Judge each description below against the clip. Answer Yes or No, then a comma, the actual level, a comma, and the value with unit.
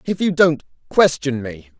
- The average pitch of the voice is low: No, medium, 145 Hz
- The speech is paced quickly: No, average, 165 wpm